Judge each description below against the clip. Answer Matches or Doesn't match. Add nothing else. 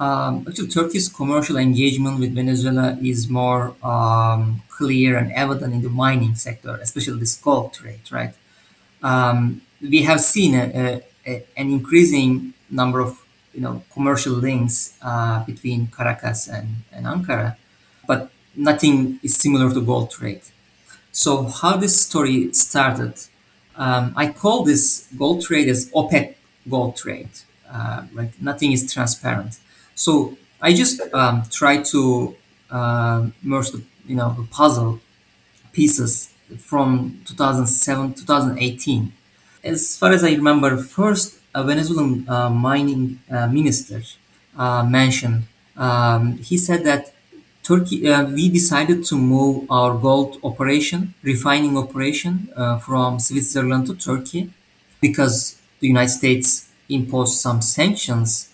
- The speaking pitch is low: Matches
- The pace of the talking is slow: Matches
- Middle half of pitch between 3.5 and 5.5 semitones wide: Doesn't match